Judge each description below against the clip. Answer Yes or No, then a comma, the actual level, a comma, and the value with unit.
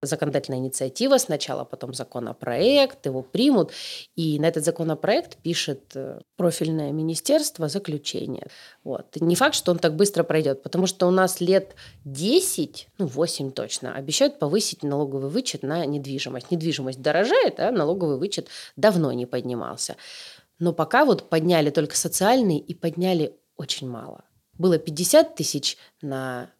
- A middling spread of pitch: Yes, average, 4.6 semitones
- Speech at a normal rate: Yes, average, 135 wpm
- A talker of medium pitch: Yes, medium, 160 Hz